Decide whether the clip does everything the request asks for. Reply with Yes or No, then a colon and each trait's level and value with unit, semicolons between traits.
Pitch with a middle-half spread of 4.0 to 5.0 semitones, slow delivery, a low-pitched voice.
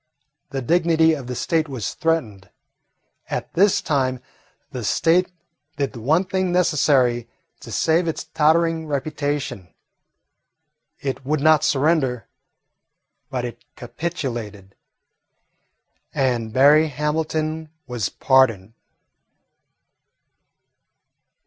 No: average, 4.5 semitones; slow, 95 wpm; medium, 145 Hz